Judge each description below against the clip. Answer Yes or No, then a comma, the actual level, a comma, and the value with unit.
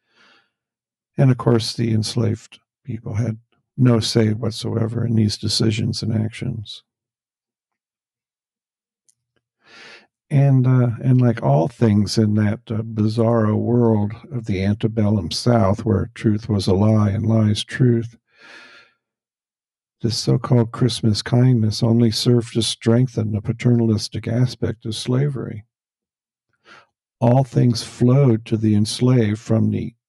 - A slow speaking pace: Yes, slow, 120 wpm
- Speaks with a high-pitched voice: No, low, 115 Hz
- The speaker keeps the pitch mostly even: Yes, narrow, 1.3 semitones